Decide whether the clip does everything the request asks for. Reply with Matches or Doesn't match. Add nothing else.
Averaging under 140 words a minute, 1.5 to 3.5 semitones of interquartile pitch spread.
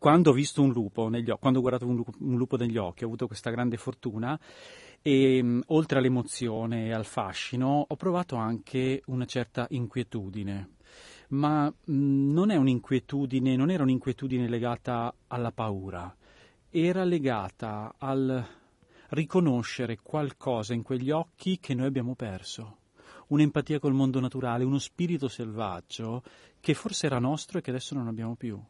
Doesn't match